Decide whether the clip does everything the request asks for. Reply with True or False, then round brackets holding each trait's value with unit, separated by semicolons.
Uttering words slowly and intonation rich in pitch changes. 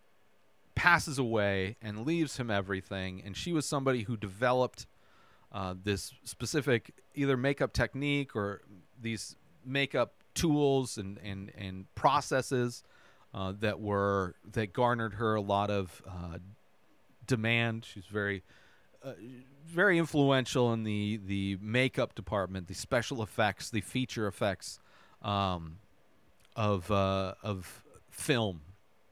False (120 wpm; 4.6 semitones)